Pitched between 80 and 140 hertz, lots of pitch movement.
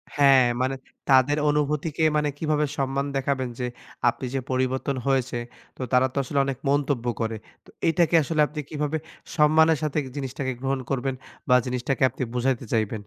No: low, 135 Hz; narrow, 2.4 semitones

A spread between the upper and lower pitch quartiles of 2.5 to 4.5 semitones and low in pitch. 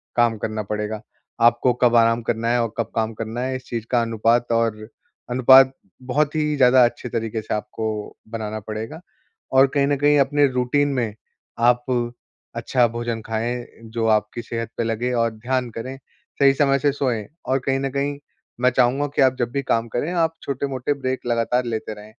Yes: average, 2.8 semitones; low, 120 Hz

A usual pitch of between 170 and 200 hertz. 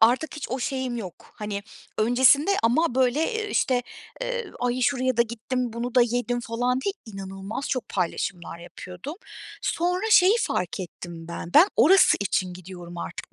No: high, 240 Hz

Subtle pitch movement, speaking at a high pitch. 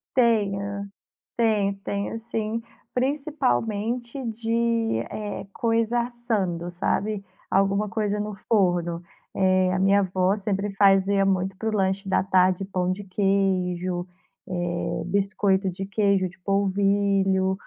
Yes: narrow, 2.2 semitones; high, 200 Hz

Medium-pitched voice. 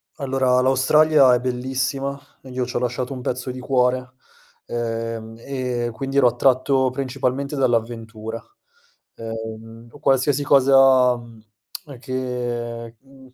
No: low, 125 Hz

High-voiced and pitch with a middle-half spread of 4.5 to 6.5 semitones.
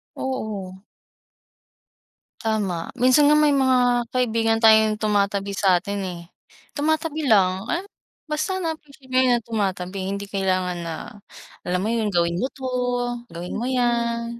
Yes: high, 220 Hz; average, 4.9 semitones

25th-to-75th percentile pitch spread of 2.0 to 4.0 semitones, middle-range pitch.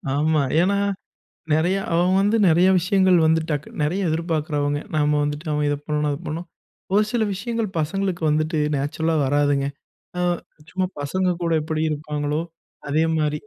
Yes: average, 3.6 semitones; medium, 160 Hz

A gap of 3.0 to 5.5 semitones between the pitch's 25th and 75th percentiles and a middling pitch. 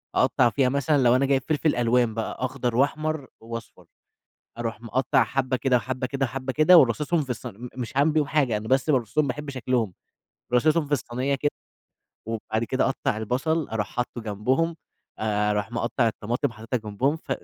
No: average, 3.4 semitones; low, 130 Hz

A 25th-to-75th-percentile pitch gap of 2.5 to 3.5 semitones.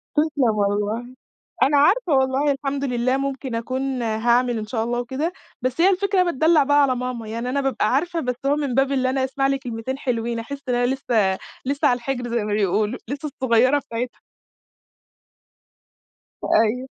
Yes: average, 3.0 semitones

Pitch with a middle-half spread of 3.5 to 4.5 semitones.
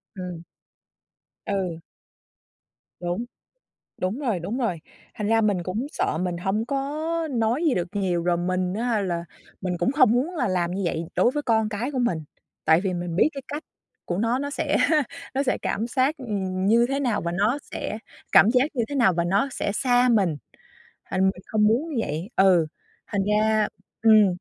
No: average, 5.2 semitones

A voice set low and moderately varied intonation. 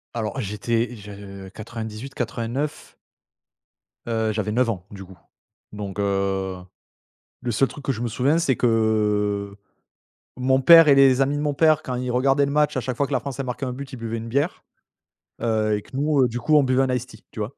Yes: low, 120 Hz; average, 4.2 semitones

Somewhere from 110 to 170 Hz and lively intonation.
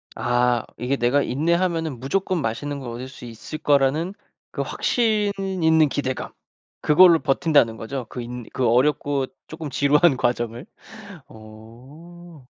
No: medium, 140 Hz; average, 4.9 semitones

